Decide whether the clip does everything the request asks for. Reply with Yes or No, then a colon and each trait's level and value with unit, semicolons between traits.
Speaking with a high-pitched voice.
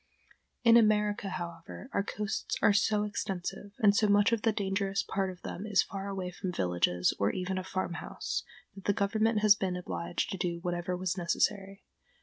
Yes: high, 195 Hz